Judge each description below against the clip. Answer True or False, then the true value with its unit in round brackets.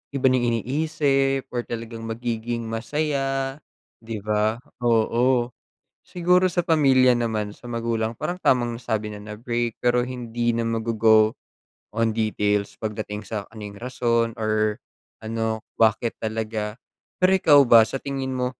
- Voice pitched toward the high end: False (115 Hz)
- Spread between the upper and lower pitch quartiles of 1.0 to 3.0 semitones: True (2.7 semitones)